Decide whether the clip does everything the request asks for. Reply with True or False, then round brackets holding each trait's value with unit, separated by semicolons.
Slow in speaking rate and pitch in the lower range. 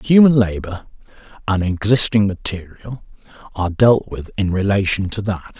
True (130 wpm; 100 Hz)